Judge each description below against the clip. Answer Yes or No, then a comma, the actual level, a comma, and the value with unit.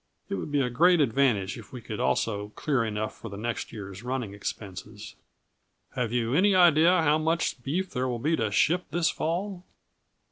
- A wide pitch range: Yes, wide, 7.0 semitones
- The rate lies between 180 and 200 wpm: Yes, average, 185 wpm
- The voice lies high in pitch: No, low, 125 Hz